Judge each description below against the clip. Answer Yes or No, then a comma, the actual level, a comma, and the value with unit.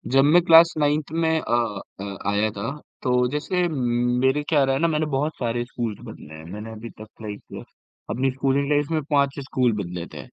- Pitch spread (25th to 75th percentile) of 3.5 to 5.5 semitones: Yes, average, 4.8 semitones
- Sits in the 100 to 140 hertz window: Yes, low, 135 Hz